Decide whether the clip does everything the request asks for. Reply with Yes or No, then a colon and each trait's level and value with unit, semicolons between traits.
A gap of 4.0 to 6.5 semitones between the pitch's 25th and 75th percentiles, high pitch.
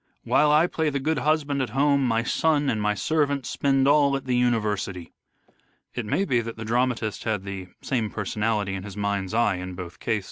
No: average, 5.1 semitones; low, 120 Hz